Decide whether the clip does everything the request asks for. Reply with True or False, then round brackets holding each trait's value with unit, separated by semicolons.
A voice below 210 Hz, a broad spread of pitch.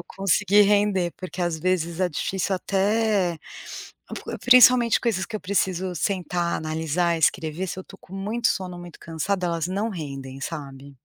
False (185 Hz; 3.3 semitones)